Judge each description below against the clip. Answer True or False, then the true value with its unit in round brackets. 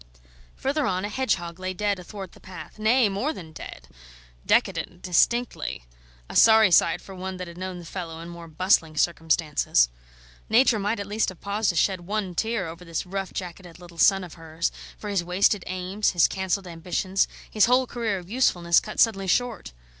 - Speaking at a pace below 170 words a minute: False (185 wpm)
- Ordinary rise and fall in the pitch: True (3.4 semitones)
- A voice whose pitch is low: False (185 Hz)